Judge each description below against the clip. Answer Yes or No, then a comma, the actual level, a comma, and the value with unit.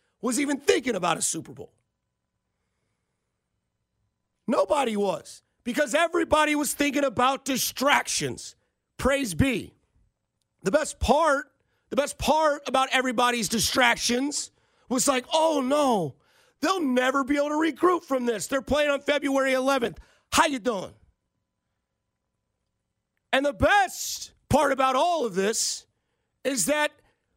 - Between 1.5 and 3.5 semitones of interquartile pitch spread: Yes, average, 3.1 semitones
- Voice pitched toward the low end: No, very high, 275 Hz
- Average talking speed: No, slow, 125 wpm